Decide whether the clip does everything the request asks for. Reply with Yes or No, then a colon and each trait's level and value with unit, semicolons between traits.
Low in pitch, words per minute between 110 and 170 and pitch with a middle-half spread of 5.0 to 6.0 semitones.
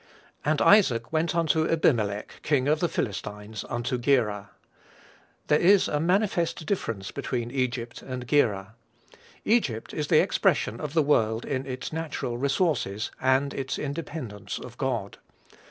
Yes: low, 130 Hz; average, 140 wpm; average, 5.3 semitones